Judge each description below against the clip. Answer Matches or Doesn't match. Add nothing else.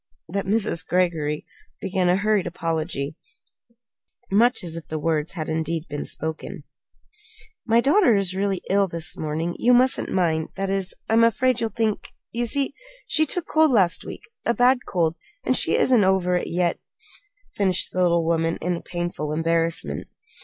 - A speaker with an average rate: Matches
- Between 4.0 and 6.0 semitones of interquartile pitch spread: Matches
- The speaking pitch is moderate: Matches